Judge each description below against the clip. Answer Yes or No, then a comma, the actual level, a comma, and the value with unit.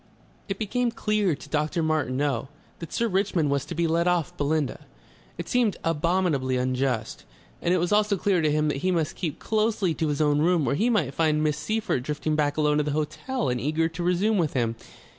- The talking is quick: Yes, fast, 210 wpm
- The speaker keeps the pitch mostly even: No, average, 4.1 semitones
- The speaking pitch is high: No, medium, 155 Hz